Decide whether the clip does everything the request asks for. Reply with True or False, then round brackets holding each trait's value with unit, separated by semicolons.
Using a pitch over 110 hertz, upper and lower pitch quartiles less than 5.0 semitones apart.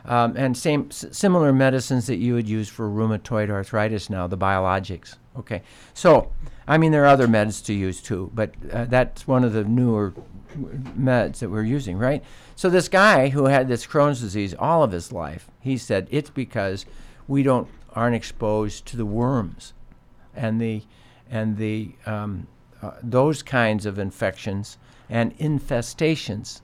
True (120 Hz; 3.7 semitones)